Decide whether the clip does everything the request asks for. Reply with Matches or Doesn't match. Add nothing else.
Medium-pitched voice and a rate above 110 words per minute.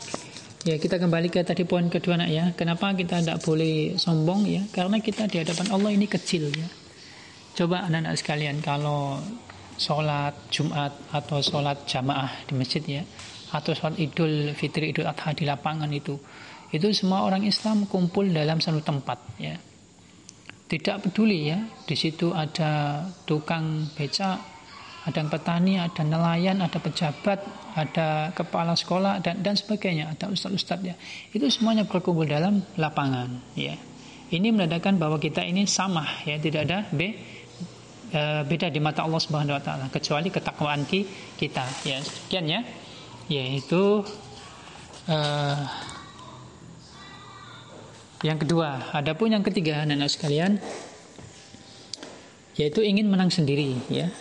Matches